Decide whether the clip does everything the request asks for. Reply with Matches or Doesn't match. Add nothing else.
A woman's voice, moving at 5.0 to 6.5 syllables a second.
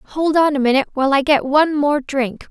Matches